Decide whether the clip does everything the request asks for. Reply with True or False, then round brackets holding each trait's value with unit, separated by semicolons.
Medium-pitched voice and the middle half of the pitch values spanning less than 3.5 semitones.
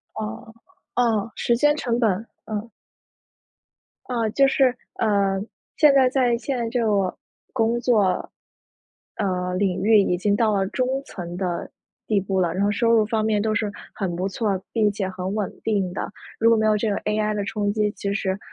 False (210 Hz; 3.0 semitones)